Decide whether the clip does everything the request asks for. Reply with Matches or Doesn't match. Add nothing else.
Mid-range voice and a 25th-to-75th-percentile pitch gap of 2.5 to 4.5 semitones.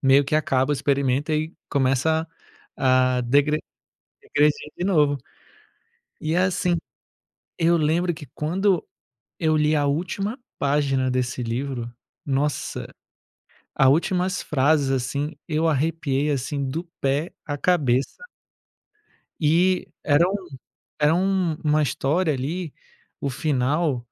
Matches